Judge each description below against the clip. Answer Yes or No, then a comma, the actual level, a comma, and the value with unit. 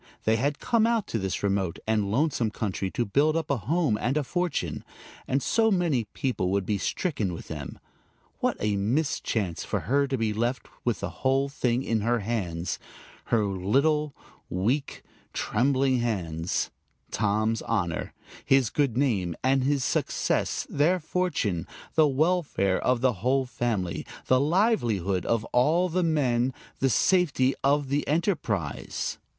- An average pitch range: No, wide, 6.0 semitones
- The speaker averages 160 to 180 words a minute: No, average, 150 wpm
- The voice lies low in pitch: Yes, low, 125 Hz